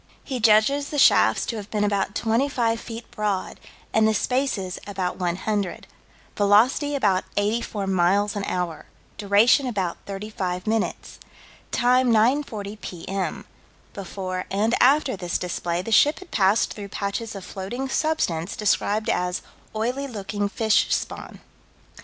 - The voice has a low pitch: No, high, 210 Hz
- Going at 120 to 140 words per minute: Yes, slow, 135 wpm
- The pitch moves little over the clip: No, average, 3.5 semitones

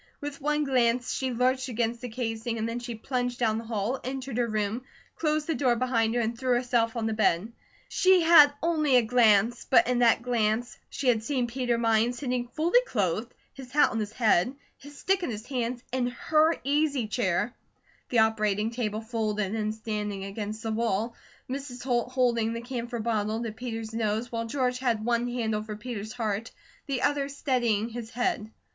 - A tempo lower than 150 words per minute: No, average, 190 wpm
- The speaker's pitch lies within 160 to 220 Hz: No, high, 235 Hz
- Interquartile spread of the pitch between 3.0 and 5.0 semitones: No, narrow, 2.5 semitones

